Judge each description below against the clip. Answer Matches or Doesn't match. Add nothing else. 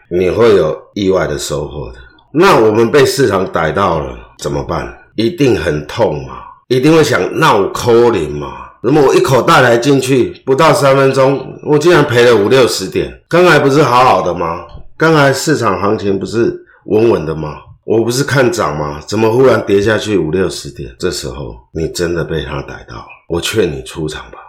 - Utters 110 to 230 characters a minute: Doesn't match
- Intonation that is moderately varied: Doesn't match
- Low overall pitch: Matches